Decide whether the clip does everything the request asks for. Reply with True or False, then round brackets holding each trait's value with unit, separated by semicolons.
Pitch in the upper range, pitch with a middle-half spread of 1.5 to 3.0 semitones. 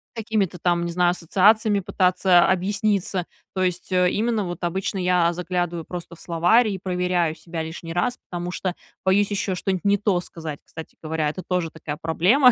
False (180 Hz; 2.4 semitones)